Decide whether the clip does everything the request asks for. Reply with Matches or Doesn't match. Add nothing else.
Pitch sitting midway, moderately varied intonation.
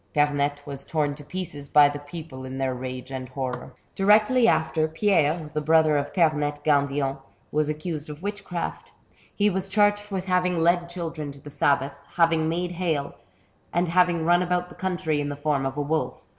Matches